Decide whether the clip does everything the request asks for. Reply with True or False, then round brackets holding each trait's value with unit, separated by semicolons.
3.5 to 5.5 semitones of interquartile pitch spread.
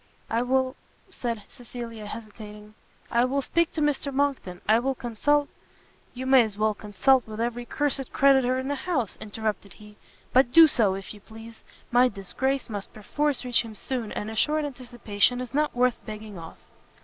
True (3.8 semitones)